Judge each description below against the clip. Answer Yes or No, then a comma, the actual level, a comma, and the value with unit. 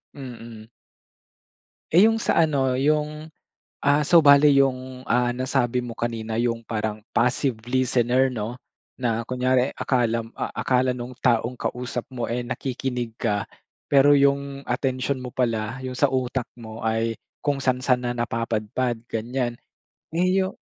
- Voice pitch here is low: Yes, low, 125 Hz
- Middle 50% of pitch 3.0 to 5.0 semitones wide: No, narrow, 2.5 semitones